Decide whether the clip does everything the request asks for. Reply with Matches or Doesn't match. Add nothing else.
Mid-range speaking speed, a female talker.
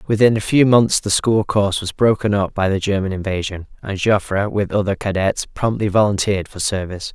Doesn't match